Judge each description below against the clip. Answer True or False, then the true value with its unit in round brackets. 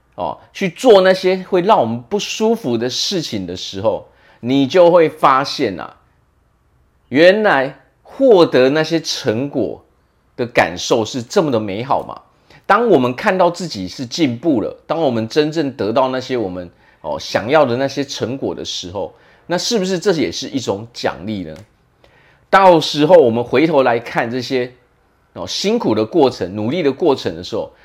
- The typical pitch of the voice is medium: True (150 Hz)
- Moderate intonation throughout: False (7.2 semitones)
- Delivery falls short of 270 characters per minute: True (240 characters per minute)